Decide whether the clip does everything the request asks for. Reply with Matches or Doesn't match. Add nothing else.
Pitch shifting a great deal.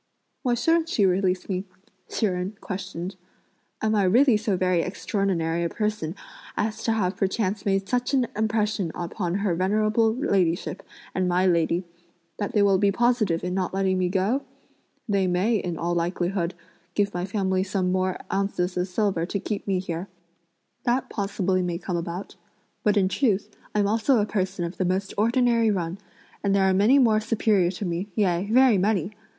Doesn't match